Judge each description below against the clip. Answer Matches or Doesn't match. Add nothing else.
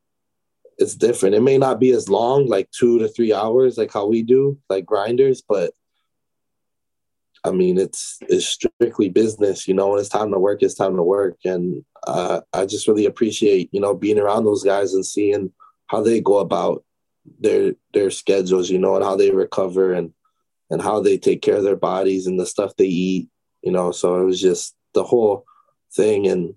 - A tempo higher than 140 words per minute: Matches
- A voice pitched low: Matches